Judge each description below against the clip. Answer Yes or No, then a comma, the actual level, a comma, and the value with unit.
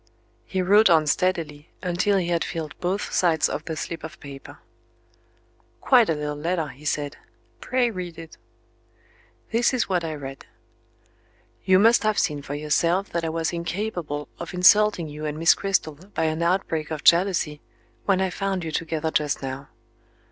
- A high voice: No, medium, 165 Hz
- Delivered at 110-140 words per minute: No, average, 170 wpm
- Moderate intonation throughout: Yes, average, 3.7 semitones